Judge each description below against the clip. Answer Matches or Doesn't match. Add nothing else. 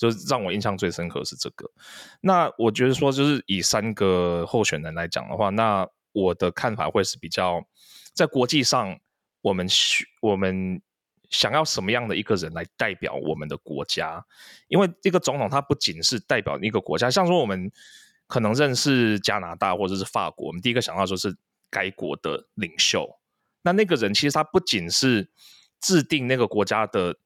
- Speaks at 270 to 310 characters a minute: Matches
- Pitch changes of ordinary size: Doesn't match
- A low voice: Matches